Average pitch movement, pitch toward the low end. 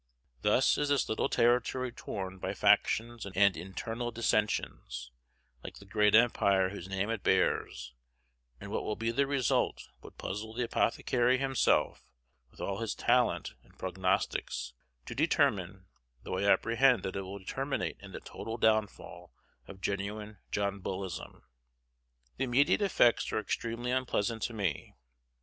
Yes: average, 3.9 semitones; low, 110 Hz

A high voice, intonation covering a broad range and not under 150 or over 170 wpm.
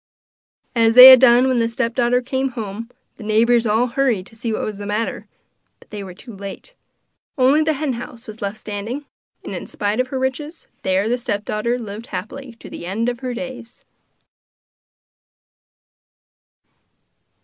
No: high, 235 Hz; average, 3.3 semitones; average, 165 wpm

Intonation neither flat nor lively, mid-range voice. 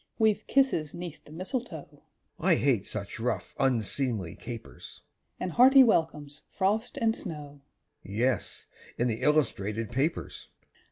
No: wide, 7.6 semitones; medium, 150 Hz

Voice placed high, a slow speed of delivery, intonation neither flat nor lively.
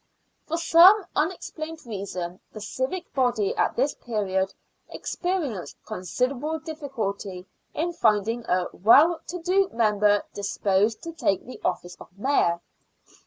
No: high, 240 Hz; slow, 120 wpm; wide, 8.1 semitones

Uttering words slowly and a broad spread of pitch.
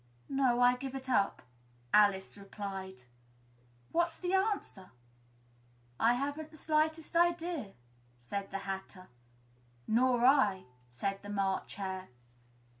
Yes: slow, 115 wpm; wide, 7.7 semitones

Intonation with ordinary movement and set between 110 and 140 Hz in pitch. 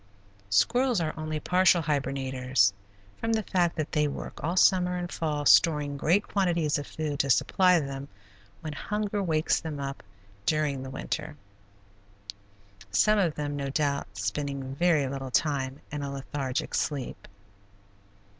No: average, 4.0 semitones; medium, 150 Hz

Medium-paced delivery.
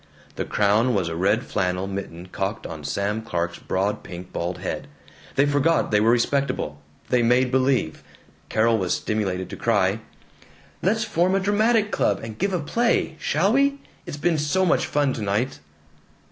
Yes: average, 165 wpm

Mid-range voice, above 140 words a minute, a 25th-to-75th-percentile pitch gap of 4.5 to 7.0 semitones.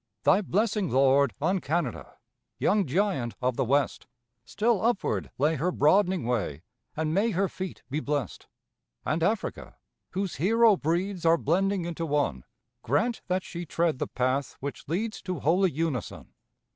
Yes: medium, 170 Hz; average, 150 wpm; wide, 5.6 semitones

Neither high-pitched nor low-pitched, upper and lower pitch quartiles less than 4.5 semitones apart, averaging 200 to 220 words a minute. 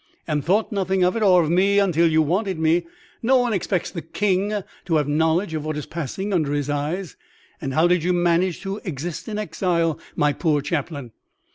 Yes: medium, 170 Hz; average, 3.6 semitones; fast, 205 wpm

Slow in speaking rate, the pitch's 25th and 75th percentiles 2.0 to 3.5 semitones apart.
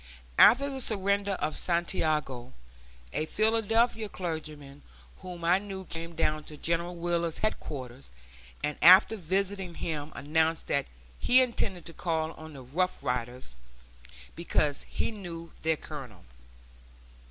No: slow, 125 wpm; average, 4.1 semitones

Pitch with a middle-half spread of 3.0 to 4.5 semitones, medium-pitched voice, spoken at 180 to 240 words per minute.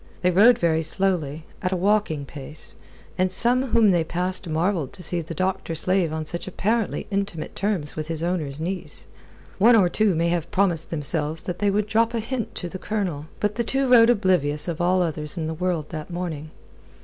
Yes: average, 4.0 semitones; medium, 180 Hz; average, 200 wpm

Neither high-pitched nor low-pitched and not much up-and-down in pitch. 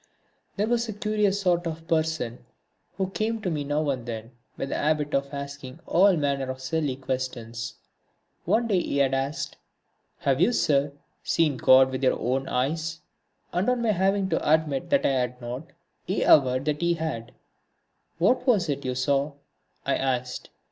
No: medium, 145 Hz; average, 5.2 semitones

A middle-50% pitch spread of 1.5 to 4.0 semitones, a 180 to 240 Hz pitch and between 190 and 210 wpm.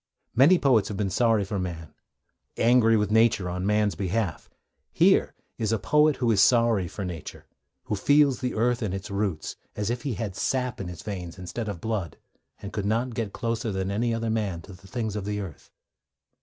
No: average, 3.2 semitones; low, 105 Hz; average, 195 wpm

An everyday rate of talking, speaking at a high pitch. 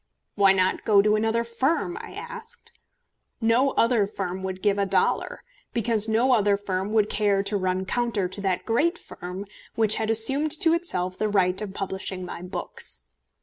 Yes: average, 175 wpm; high, 210 Hz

